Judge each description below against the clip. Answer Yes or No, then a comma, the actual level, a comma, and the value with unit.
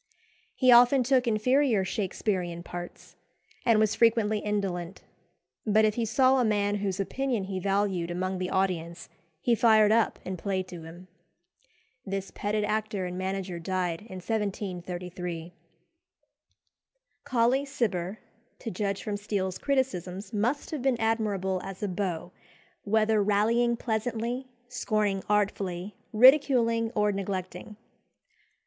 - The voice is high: Yes, high, 205 Hz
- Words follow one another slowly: Yes, slow, 125 wpm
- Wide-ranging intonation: No, average, 3.6 semitones